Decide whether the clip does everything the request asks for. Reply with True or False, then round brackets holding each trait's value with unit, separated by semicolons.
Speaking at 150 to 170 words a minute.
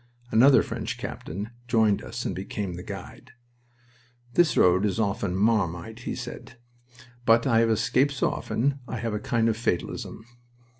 True (155 wpm)